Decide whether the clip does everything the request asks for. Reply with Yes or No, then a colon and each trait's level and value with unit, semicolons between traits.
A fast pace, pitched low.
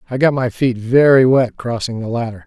Yes: fast, 220 wpm; low, 120 Hz